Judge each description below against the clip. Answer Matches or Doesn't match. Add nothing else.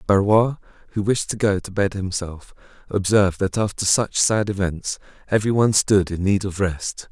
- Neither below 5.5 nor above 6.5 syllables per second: Doesn't match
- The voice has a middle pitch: Doesn't match